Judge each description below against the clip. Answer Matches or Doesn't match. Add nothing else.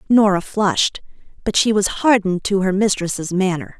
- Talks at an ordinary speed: Matches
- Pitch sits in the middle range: Doesn't match